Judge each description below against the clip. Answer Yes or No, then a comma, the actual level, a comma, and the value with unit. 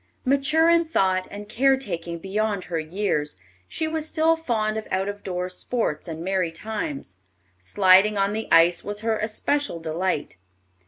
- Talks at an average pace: Yes, average, 155 wpm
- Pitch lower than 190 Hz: No, high, 205 Hz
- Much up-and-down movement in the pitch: Yes, wide, 5.9 semitones